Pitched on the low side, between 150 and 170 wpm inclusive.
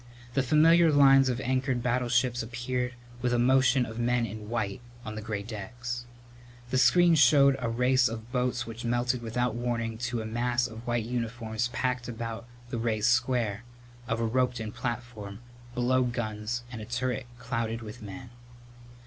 Yes: low, 120 Hz; average, 165 wpm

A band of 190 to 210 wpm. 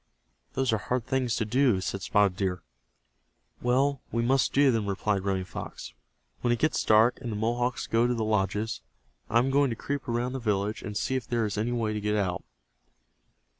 Yes: fast, 205 wpm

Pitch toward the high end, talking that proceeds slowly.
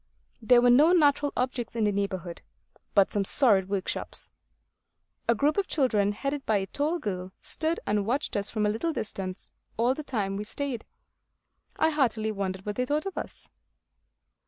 No: high, 230 Hz; average, 175 wpm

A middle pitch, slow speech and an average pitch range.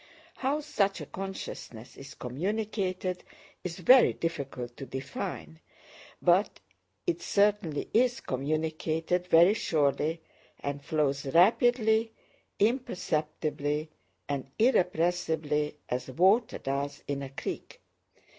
No: medium, 165 Hz; slow, 100 wpm; wide, 6.0 semitones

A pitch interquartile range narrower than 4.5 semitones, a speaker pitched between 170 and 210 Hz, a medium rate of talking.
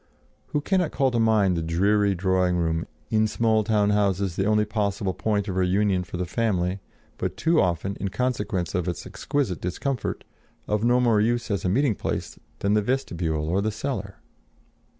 No: average, 3.5 semitones; low, 100 Hz; average, 180 wpm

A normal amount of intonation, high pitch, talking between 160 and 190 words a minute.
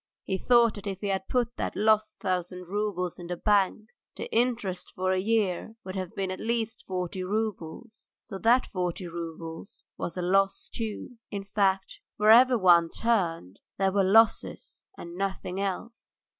Yes: average, 3.2 semitones; high, 195 Hz; average, 165 wpm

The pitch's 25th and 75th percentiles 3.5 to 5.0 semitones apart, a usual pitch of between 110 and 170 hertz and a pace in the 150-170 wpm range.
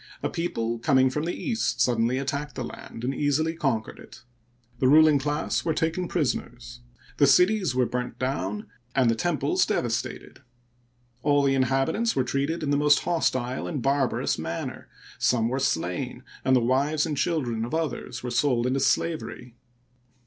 Yes: average, 4.0 semitones; low, 135 Hz; average, 165 wpm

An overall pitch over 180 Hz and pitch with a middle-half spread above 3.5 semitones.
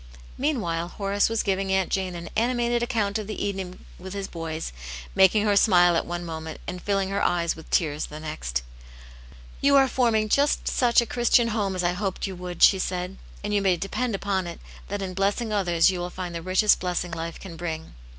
No: high, 190 Hz; average, 3.2 semitones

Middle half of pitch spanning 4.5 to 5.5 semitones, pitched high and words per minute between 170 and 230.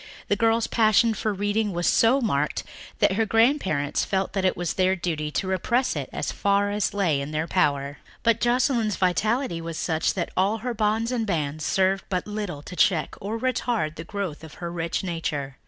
Yes: average, 5.1 semitones; high, 195 Hz; average, 195 wpm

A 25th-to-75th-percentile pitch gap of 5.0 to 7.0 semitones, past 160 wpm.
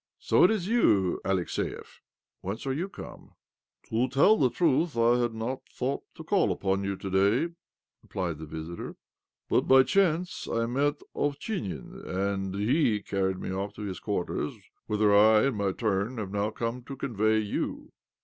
Yes: wide, 5.6 semitones; average, 180 wpm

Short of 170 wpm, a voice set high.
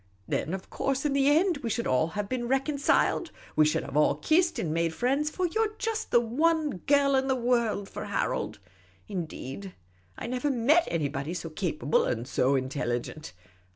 No: average, 180 wpm; high, 235 Hz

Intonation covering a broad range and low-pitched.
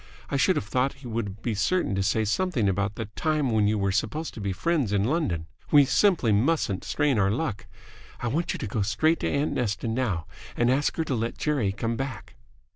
Yes: wide, 6.0 semitones; low, 115 Hz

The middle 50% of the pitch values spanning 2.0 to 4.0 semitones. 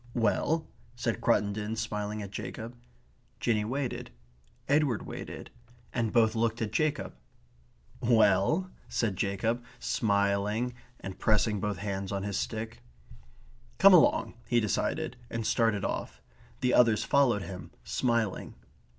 Yes: average, 2.9 semitones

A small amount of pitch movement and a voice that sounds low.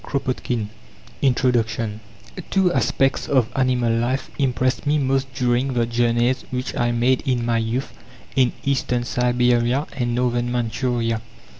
Yes: narrow, 1.7 semitones; low, 125 Hz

